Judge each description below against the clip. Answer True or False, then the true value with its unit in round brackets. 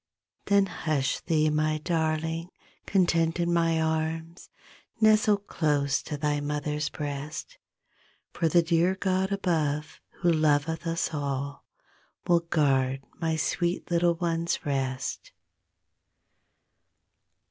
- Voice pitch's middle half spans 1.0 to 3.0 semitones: True (2.4 semitones)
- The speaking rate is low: True (105 wpm)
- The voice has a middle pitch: True (160 Hz)